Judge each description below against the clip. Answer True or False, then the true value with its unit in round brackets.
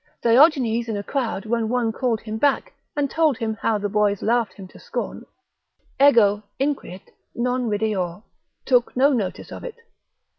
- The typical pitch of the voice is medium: False (230 Hz)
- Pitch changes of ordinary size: True (3.5 semitones)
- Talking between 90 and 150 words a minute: False (160 wpm)